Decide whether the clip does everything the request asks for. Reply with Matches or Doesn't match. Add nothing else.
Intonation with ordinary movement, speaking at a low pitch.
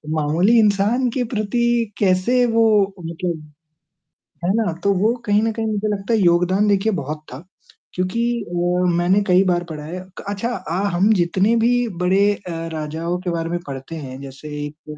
Doesn't match